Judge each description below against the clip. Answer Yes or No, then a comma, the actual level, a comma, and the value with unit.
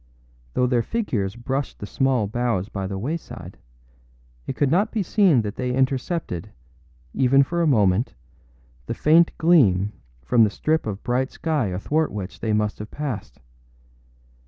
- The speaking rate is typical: Yes, average, 155 wpm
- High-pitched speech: No, low, 125 Hz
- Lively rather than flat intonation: Yes, wide, 6.3 semitones